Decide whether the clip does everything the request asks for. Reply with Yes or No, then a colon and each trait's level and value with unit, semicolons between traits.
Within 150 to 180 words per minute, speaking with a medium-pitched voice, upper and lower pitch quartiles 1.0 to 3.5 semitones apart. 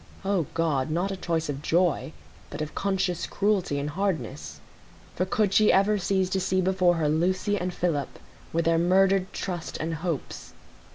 Yes: average, 170 wpm; medium, 180 Hz; average, 3.1 semitones